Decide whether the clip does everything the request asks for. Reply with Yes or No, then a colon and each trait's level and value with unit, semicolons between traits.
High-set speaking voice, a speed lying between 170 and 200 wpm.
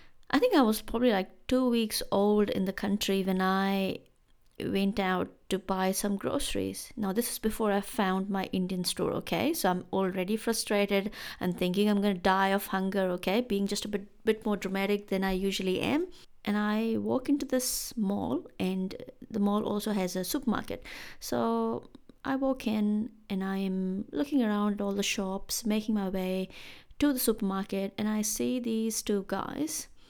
Yes: high, 205 Hz; average, 180 wpm